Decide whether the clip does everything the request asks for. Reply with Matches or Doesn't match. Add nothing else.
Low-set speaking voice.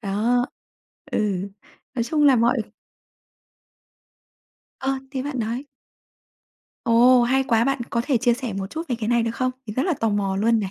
Doesn't match